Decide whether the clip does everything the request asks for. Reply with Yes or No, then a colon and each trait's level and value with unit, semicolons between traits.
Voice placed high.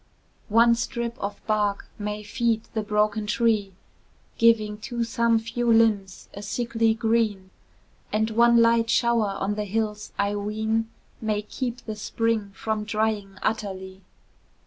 Yes: high, 220 Hz